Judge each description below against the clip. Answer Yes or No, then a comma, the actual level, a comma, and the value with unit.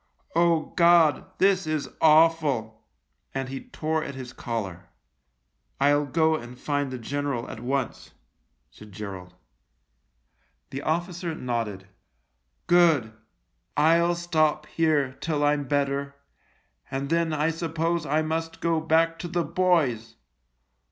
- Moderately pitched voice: Yes, medium, 150 Hz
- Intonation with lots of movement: No, average, 4.2 semitones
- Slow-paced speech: Yes, slow, 125 wpm